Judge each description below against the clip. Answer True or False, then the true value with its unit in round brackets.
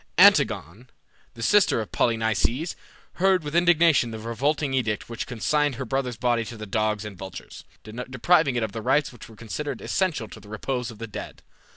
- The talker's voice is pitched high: False (120 Hz)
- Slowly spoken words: False (185 wpm)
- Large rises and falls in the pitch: False (4.9 semitones)